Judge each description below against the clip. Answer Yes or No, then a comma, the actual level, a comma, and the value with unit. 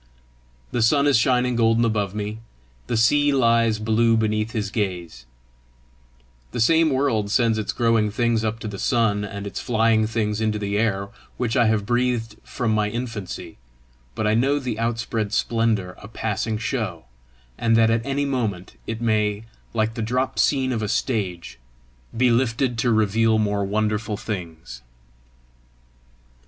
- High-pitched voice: No, low, 110 Hz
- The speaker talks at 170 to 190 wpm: No, average, 155 wpm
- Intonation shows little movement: Yes, narrow, 2.0 semitones